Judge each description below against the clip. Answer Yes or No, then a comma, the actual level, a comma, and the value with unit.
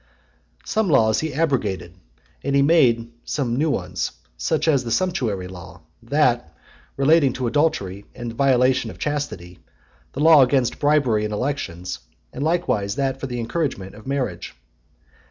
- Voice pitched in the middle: No, low, 130 Hz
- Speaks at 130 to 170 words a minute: Yes, average, 155 wpm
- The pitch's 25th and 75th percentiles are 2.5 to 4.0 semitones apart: No, average, 5.3 semitones